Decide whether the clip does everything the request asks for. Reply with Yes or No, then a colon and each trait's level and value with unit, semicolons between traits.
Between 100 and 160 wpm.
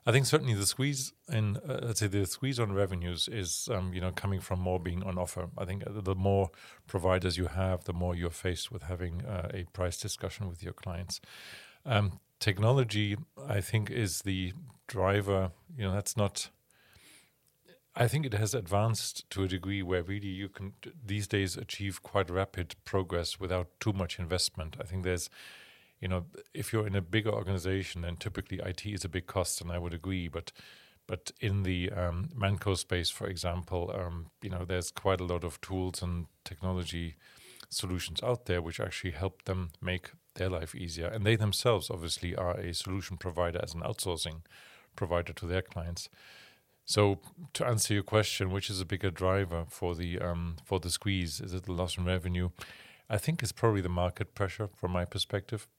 No: average, 185 wpm